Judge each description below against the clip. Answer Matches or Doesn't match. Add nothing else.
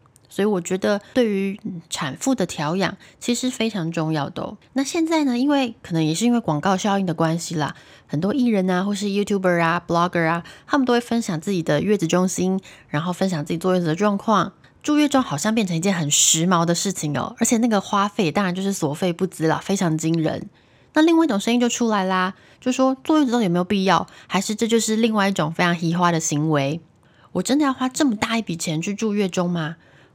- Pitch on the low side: Doesn't match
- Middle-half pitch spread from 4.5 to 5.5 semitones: Matches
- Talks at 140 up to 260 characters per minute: Doesn't match